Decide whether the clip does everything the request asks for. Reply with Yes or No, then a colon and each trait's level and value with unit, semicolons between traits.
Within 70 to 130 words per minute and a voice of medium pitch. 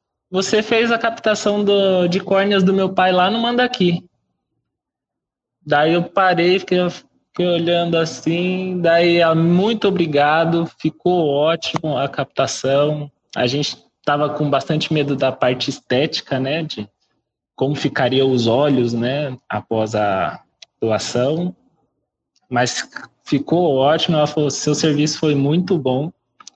Yes: average, 125 wpm; medium, 160 Hz